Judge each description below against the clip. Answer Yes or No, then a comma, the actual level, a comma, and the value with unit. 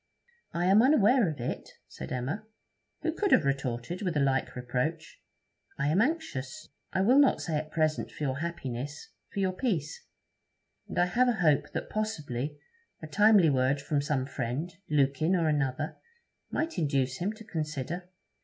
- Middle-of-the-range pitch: Yes, medium, 155 Hz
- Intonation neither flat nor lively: No, wide, 5.7 semitones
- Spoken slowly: No, average, 165 wpm